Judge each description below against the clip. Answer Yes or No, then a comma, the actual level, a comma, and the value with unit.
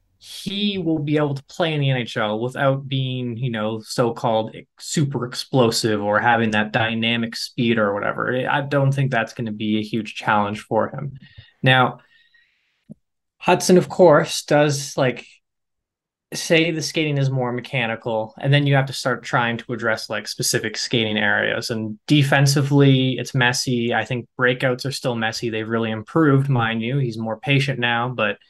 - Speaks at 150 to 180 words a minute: Yes, average, 170 wpm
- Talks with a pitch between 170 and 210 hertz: No, low, 125 Hz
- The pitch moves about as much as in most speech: Yes, average, 3.6 semitones